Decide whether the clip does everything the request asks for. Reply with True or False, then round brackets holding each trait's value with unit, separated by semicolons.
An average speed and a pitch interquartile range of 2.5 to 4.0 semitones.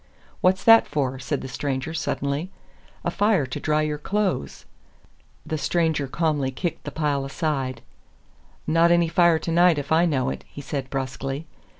True (160 wpm; 3.7 semitones)